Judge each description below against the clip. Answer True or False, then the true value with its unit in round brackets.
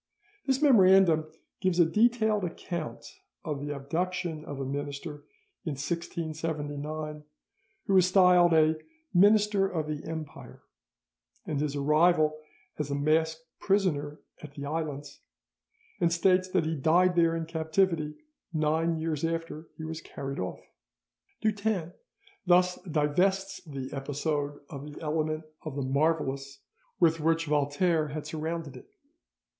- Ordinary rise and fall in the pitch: True (3.0 semitones)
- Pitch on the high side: False (160 Hz)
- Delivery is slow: True (130 wpm)